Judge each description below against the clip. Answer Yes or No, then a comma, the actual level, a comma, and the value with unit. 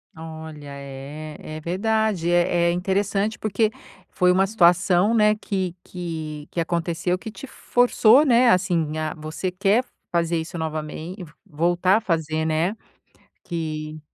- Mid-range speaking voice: Yes, medium, 175 Hz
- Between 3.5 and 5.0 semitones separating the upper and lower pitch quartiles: Yes, average, 3.8 semitones